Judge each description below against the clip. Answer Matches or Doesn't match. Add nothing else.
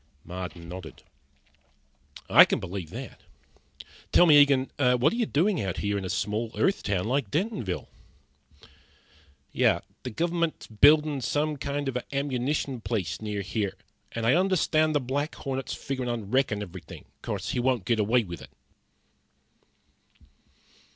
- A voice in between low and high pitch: Doesn't match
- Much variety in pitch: Matches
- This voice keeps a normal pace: Matches